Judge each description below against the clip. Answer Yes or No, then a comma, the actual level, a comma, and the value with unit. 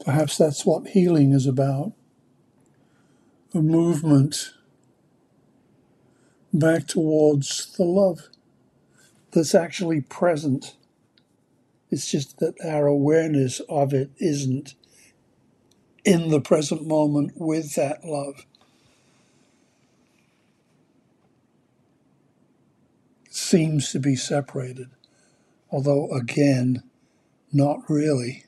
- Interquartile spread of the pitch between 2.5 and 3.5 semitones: Yes, average, 2.9 semitones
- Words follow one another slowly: Yes, slow, 80 wpm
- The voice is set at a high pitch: No, medium, 145 Hz